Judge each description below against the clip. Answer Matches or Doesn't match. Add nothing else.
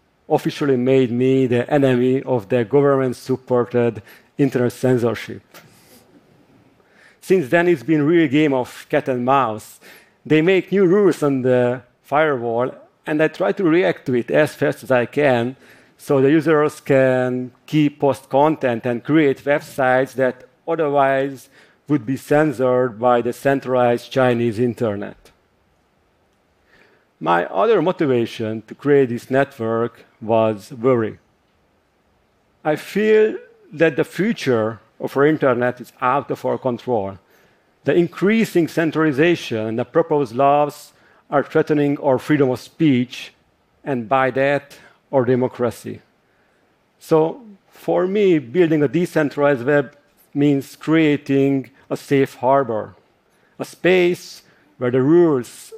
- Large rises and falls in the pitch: Doesn't match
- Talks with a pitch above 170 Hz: Doesn't match